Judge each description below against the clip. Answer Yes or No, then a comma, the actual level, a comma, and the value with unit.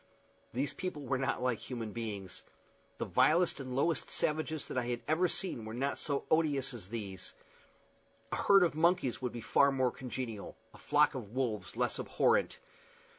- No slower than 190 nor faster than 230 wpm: No, average, 175 wpm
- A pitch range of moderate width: Yes, average, 4.7 semitones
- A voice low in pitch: Yes, low, 130 Hz